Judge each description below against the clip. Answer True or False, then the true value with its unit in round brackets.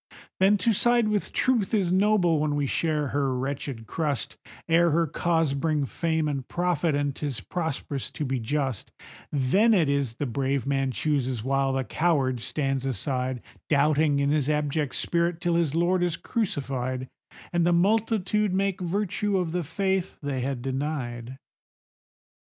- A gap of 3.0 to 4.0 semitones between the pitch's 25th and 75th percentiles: False (4.4 semitones)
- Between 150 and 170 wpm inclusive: True (160 wpm)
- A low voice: False (150 Hz)